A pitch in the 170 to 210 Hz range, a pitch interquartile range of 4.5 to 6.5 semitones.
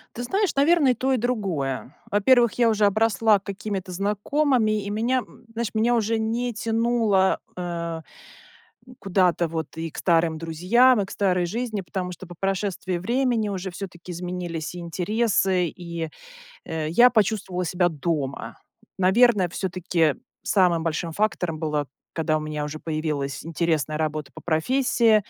Yes: medium, 185 Hz; average, 5.1 semitones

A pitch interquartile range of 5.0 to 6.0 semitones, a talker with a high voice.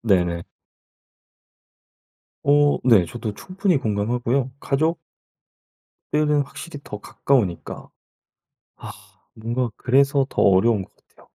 No: wide, 5.4 semitones; low, 125 Hz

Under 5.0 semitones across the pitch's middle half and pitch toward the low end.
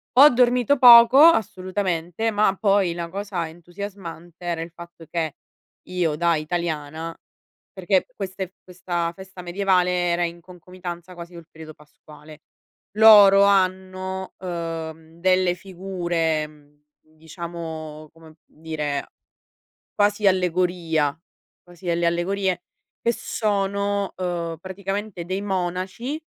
No: average, 2.7 semitones; medium, 180 Hz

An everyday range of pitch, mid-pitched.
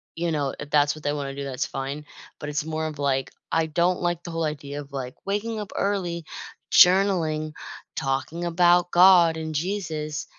Yes: average, 3.2 semitones; medium, 160 Hz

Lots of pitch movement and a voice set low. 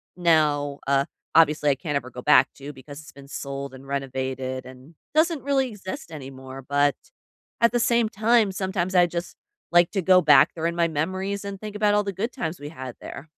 No: wide, 6.0 semitones; medium, 160 Hz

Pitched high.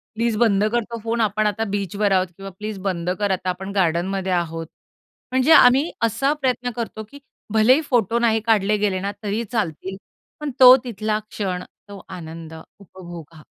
Yes: high, 205 Hz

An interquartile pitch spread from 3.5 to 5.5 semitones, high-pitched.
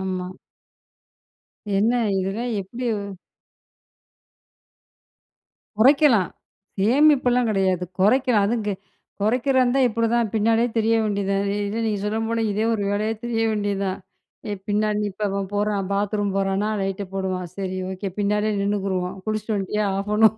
No: narrow, 2.5 semitones; high, 210 Hz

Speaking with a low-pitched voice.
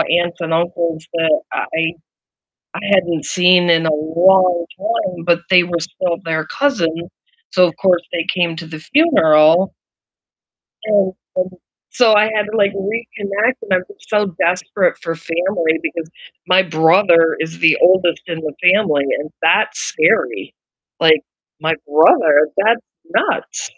No: medium, 175 Hz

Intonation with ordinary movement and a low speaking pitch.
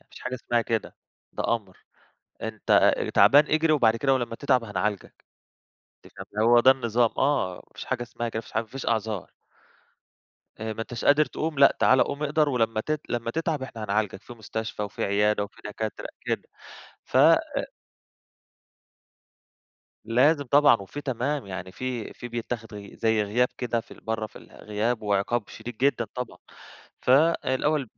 Yes: average, 3.5 semitones; low, 120 Hz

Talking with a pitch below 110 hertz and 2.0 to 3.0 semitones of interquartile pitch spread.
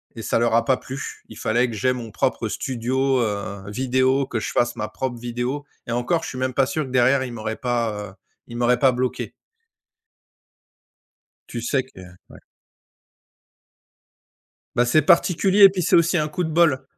No: low, 125 Hz; narrow, 2.5 semitones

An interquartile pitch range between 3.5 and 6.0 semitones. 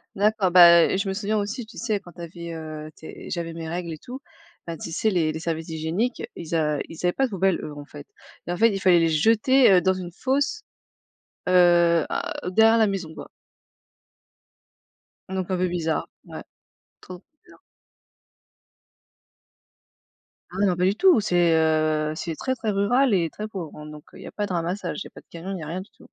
Yes: average, 4.0 semitones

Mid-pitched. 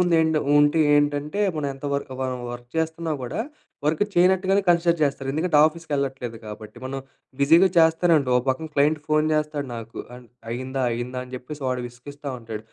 Yes: medium, 145 Hz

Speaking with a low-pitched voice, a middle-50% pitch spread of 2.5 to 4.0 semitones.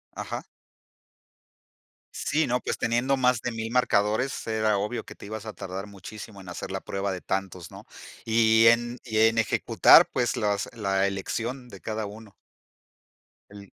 Yes: low, 110 Hz; average, 2.8 semitones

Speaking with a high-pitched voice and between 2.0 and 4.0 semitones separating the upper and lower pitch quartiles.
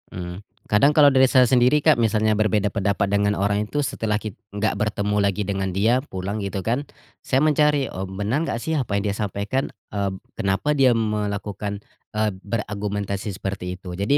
No: low, 105 Hz; average, 3.1 semitones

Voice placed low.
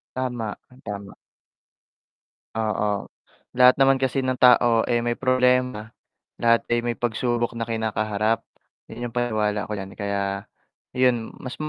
Yes: low, 115 Hz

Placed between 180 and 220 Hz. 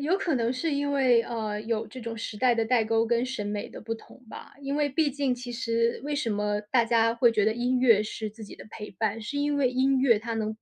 No: high, 235 Hz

